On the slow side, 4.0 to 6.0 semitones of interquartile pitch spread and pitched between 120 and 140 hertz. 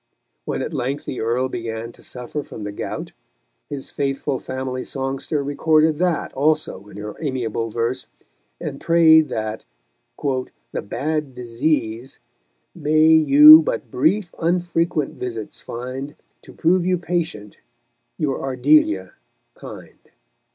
Yes: slow, 125 wpm; average, 4.5 semitones; low, 135 Hz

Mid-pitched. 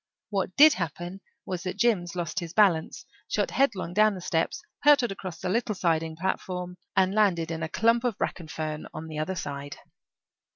Yes: medium, 180 Hz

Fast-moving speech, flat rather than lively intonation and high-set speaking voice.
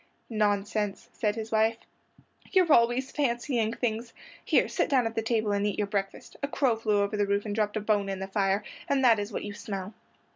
Yes: fast, 215 wpm; narrow, 2.3 semitones; high, 215 Hz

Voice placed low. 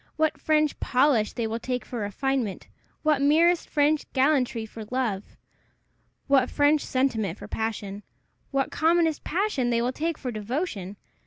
No: very high, 260 Hz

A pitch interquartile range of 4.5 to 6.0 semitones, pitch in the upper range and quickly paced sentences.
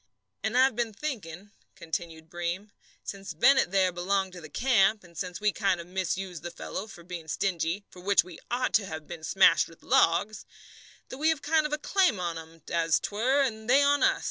Yes: wide, 5.5 semitones; high, 195 Hz; fast, 210 wpm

